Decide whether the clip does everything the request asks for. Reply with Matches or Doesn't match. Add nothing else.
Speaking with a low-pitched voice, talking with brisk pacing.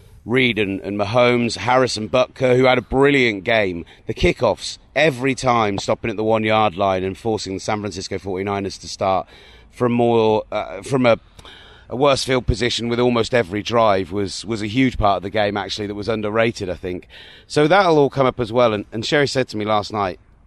Matches